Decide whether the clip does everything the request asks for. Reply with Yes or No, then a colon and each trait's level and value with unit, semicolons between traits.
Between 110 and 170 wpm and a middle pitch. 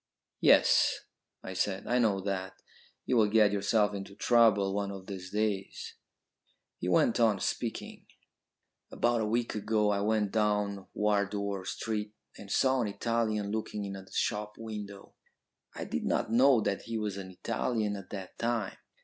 No: average, 160 wpm; low, 105 Hz